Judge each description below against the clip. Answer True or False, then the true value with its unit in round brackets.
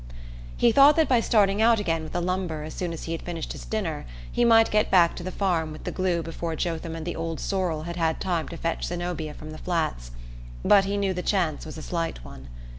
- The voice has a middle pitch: True (170 Hz)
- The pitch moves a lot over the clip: False (3.2 semitones)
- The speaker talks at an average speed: False (245 wpm)